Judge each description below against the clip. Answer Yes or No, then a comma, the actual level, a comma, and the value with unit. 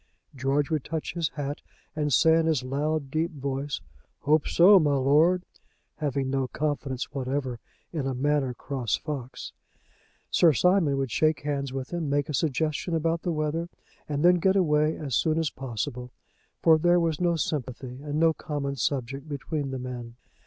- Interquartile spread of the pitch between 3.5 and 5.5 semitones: No, average, 2.9 semitones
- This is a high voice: No, medium, 145 Hz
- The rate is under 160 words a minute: No, average, 170 wpm